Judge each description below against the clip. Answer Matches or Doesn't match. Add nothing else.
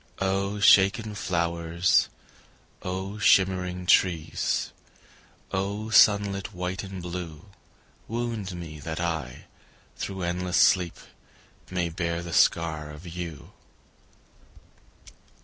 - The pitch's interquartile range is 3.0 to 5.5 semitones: Doesn't match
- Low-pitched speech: Matches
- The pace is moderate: Doesn't match